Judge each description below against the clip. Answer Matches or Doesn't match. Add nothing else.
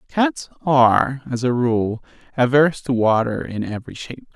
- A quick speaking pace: Doesn't match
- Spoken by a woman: Doesn't match